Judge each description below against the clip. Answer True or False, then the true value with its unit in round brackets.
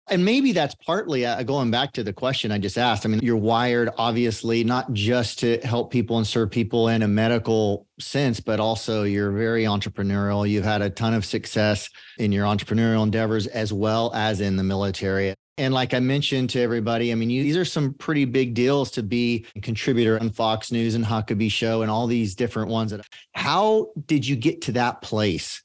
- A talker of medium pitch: False (115 Hz)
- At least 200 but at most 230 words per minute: True (205 wpm)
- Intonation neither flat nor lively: False (2.3 semitones)